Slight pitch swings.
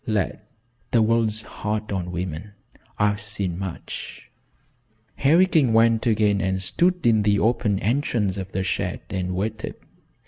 No: average, 3.0 semitones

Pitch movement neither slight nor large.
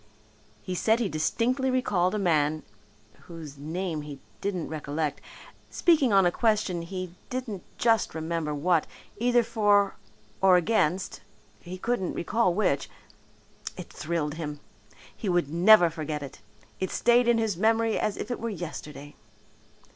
No: wide, 5.7 semitones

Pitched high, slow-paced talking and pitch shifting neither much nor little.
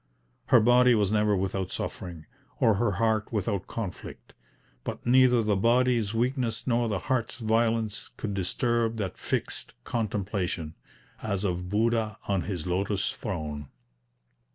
No: low, 105 Hz; slow, 130 wpm; average, 3.3 semitones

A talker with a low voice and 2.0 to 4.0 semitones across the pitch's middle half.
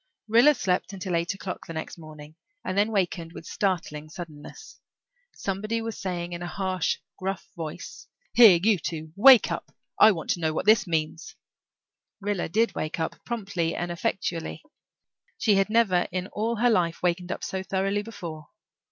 No: medium, 185 Hz; average, 3.6 semitones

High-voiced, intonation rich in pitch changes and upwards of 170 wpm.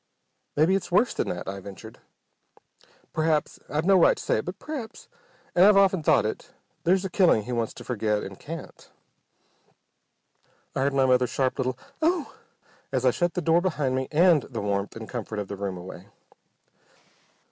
No: low, 135 Hz; wide, 8.4 semitones; average, 180 wpm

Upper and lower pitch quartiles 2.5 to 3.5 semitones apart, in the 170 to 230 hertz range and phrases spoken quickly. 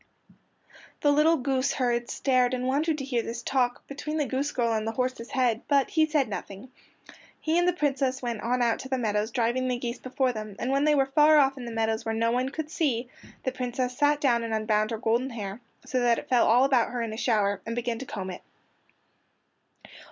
No: average, 2.9 semitones; very high, 250 Hz; fast, 225 wpm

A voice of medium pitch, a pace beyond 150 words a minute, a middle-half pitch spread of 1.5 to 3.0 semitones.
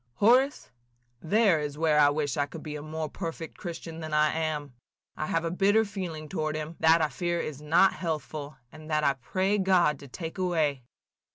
Yes: medium, 160 Hz; average, 195 wpm; average, 2.7 semitones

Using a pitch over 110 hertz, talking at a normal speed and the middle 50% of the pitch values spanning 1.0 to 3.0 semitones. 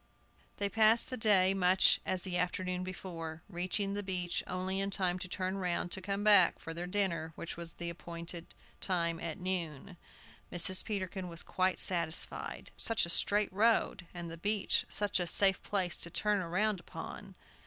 Yes: medium, 185 Hz; average, 165 wpm; narrow, 2.4 semitones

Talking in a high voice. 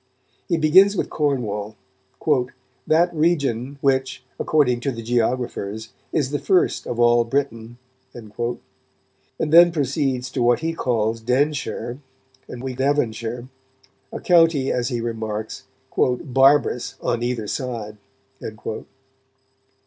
No: low, 125 Hz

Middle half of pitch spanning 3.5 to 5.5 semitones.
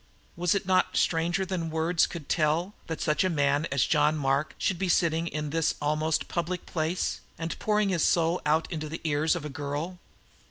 No: narrow, 2.6 semitones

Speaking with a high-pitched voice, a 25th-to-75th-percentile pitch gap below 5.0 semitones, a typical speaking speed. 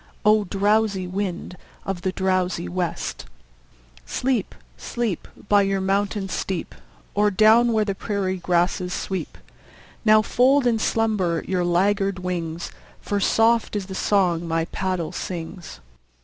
No: high, 195 Hz; average, 2.8 semitones; slow, 130 wpm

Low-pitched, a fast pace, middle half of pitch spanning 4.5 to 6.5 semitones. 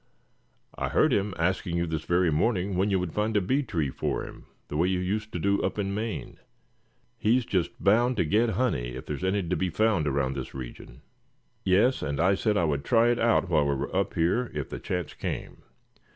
Yes: very low, 95 Hz; fast, 220 wpm; average, 5.0 semitones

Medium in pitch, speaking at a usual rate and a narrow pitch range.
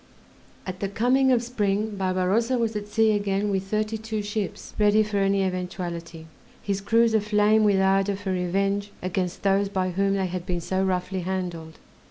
No: high, 195 Hz; average, 175 wpm; narrow, 2.2 semitones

